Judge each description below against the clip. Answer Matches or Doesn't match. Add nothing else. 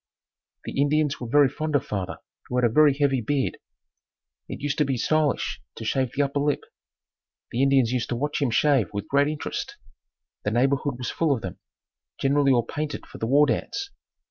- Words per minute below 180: Doesn't match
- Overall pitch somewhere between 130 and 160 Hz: Matches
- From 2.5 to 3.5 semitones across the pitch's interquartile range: Matches